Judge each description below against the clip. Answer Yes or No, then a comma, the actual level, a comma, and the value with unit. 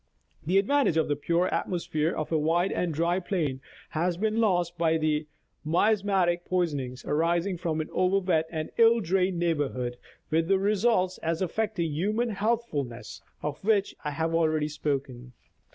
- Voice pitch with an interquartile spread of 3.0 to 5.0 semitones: Yes, average, 3.8 semitones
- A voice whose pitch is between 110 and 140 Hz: No, medium, 170 Hz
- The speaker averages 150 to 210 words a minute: Yes, average, 155 wpm